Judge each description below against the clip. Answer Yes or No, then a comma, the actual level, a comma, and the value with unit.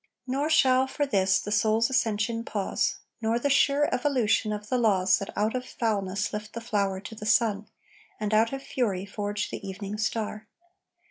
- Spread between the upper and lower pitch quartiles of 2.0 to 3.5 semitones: Yes, average, 2.8 semitones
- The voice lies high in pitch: Yes, high, 215 Hz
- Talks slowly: No, average, 175 wpm